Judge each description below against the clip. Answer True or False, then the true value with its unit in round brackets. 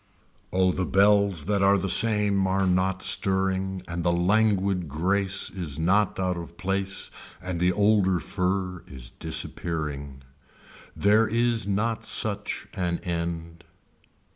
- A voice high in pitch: False (95 Hz)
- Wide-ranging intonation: False (2.6 semitones)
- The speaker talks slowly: True (130 wpm)